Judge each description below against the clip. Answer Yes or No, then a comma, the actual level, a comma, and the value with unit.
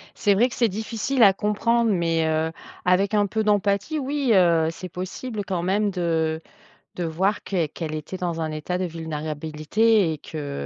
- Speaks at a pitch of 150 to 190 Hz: Yes, medium, 185 Hz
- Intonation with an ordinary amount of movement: Yes, average, 4.6 semitones